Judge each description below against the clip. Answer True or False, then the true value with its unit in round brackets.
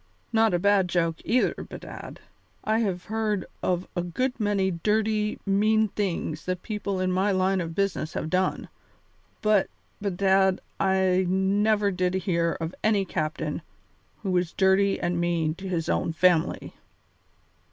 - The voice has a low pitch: False (190 Hz)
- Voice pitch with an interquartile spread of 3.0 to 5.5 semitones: False (2.6 semitones)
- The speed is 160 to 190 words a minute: False (145 wpm)